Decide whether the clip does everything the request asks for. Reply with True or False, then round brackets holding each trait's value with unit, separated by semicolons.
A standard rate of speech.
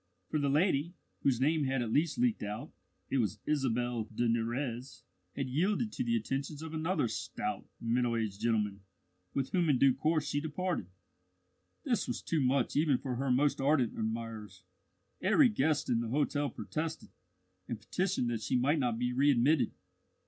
True (170 wpm)